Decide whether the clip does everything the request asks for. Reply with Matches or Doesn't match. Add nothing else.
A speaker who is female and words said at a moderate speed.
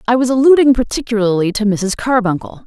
Matches